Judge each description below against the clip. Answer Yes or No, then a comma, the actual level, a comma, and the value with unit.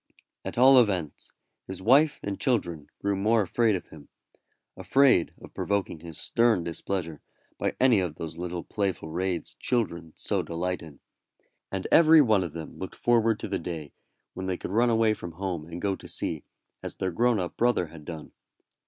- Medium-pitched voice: No, very low, 95 Hz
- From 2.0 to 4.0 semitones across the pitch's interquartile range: No, average, 5.2 semitones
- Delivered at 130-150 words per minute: No, average, 180 wpm